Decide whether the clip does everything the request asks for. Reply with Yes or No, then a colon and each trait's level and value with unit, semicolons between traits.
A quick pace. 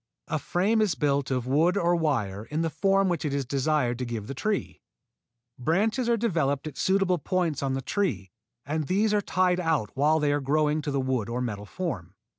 Yes: fast, 210 wpm